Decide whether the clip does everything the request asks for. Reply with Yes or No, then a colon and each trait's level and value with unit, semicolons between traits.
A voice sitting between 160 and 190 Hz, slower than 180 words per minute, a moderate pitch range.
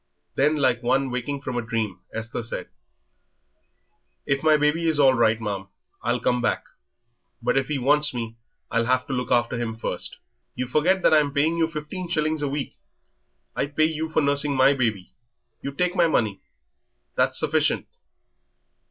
No: low, 135 Hz; average, 170 wpm; average, 4.2 semitones